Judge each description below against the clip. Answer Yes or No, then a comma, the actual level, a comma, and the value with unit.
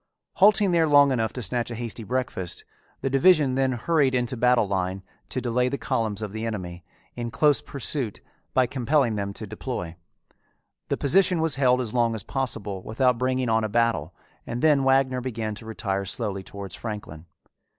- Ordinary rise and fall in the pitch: Yes, average, 3.8 semitones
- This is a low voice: Yes, low, 120 Hz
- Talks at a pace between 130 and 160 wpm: No, average, 180 wpm